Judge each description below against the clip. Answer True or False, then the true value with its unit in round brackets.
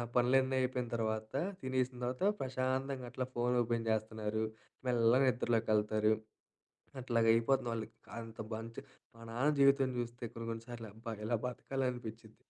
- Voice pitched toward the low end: True (120 Hz)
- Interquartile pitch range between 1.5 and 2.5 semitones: True (2.2 semitones)